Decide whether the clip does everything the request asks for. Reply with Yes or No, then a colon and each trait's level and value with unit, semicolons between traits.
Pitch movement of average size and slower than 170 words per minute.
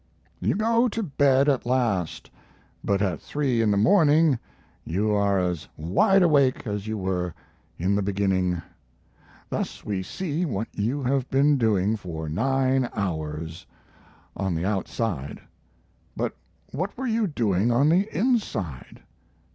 No: wide, 7.3 semitones; average, 140 wpm